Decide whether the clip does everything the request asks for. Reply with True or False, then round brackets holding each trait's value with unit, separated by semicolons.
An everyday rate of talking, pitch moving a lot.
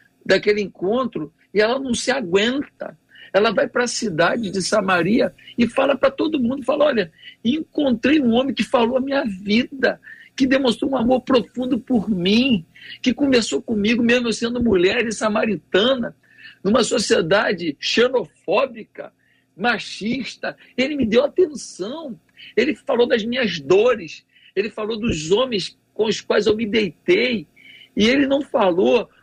False (150 wpm; 4.1 semitones)